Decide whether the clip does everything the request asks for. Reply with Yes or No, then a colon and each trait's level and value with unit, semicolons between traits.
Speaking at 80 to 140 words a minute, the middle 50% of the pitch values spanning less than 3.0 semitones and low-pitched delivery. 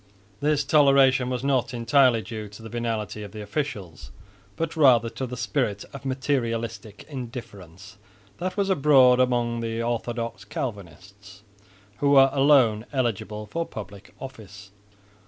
No: slow, 135 wpm; average, 4.2 semitones; low, 120 Hz